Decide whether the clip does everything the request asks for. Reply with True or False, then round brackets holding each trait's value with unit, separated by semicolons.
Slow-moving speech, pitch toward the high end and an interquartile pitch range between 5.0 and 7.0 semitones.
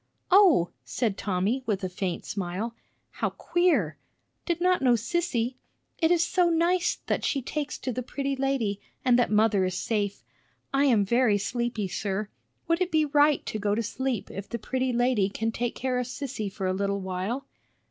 False (185 wpm; 240 Hz; 5.5 semitones)